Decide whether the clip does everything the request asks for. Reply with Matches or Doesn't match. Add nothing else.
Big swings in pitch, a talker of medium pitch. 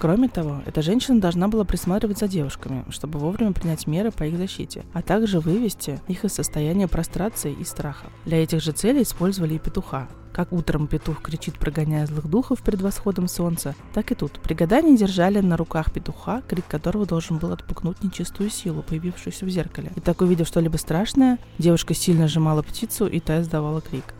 Doesn't match